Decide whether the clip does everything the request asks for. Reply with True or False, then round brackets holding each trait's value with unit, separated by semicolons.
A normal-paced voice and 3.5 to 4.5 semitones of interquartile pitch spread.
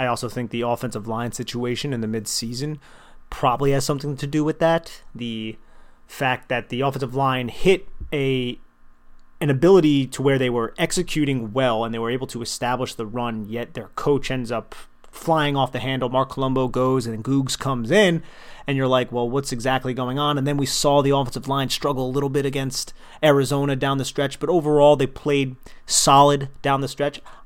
False (195 wpm; 2.7 semitones)